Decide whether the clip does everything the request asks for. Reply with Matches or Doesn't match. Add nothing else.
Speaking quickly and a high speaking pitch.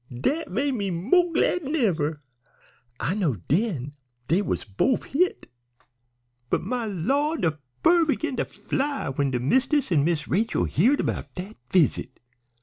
Doesn't match